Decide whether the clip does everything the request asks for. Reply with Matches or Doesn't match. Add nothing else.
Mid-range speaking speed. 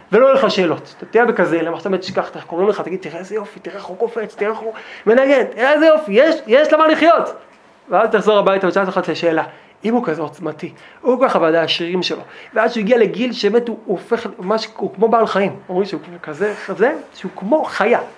Doesn't match